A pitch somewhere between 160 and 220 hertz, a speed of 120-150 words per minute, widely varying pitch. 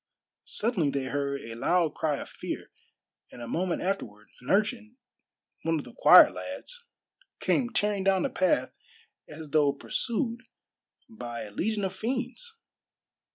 Yes: medium, 185 Hz; average, 145 wpm; wide, 8.1 semitones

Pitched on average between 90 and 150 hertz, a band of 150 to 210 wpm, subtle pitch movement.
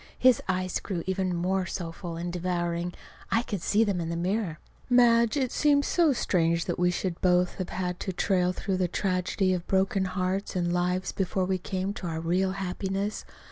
No: medium, 185 Hz; average, 190 wpm; narrow, 1.8 semitones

